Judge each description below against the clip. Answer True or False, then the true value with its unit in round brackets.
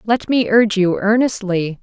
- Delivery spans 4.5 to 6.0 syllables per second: True (4.7 syllables/s)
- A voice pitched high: True (210 Hz)